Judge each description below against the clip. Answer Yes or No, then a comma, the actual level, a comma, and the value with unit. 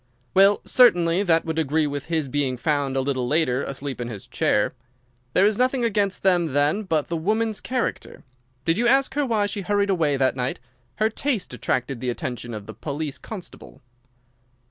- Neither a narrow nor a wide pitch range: No, wide, 7.0 semitones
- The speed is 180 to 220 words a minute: Yes, average, 185 wpm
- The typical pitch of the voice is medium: Yes, medium, 160 Hz